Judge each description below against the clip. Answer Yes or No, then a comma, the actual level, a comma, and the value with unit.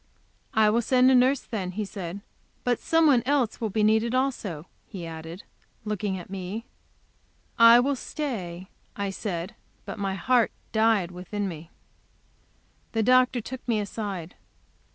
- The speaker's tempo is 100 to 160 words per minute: Yes, average, 150 wpm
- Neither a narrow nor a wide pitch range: Yes, average, 4.6 semitones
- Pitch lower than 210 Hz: No, high, 215 Hz